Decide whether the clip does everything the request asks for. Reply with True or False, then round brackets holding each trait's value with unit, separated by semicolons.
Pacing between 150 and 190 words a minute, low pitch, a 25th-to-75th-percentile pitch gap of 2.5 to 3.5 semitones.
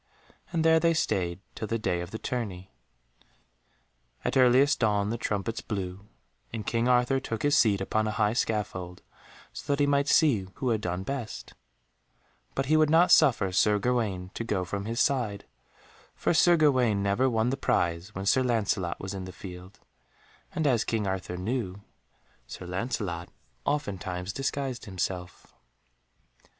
False (160 wpm; 110 Hz; 5.4 semitones)